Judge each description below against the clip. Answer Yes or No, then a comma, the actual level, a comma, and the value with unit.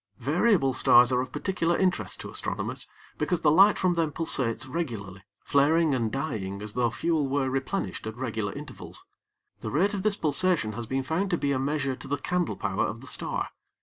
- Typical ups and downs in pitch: No, wide, 5.7 semitones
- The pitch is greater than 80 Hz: Yes, medium, 140 Hz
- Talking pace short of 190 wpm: No, average, 195 wpm